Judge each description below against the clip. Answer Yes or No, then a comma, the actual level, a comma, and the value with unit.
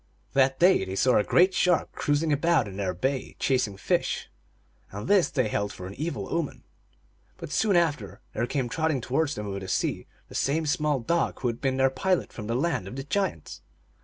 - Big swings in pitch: Yes, wide, 7.2 semitones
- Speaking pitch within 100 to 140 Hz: Yes, low, 135 Hz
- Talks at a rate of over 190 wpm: Yes, fast, 205 wpm